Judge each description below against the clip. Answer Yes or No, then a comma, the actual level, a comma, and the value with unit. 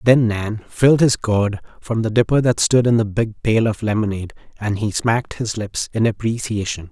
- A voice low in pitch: Yes, low, 110 Hz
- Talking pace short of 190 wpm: No, average, 200 wpm